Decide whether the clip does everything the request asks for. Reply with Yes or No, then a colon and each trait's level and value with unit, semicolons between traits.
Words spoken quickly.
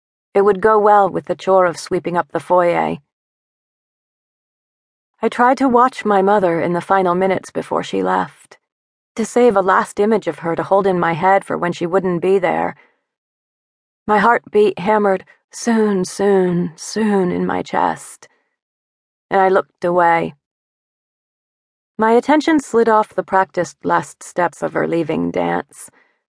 No: average, 155 wpm